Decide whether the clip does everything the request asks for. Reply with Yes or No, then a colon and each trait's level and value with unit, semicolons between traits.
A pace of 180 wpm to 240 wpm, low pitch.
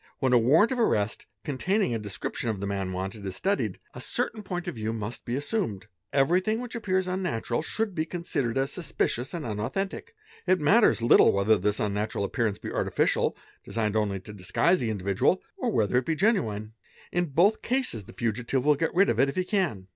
Yes: average, 200 wpm; low, 130 Hz